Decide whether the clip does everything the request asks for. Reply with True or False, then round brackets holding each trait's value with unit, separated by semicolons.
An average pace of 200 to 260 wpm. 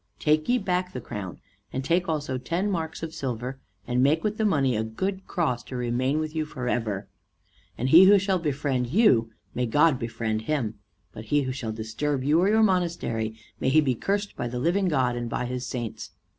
True (205 wpm)